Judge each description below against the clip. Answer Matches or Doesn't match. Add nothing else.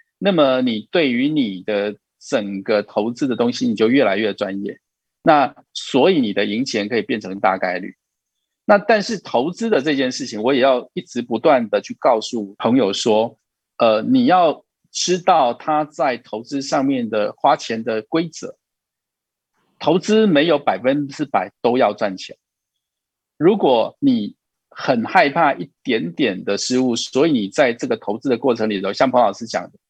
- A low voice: Doesn't match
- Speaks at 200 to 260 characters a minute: Matches